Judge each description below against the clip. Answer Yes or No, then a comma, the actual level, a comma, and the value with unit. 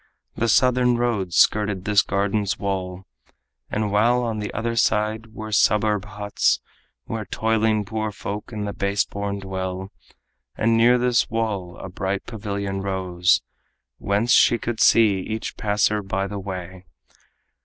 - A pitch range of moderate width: No, narrow, 2.3 semitones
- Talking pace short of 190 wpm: Yes, average, 140 wpm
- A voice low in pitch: Yes, low, 105 Hz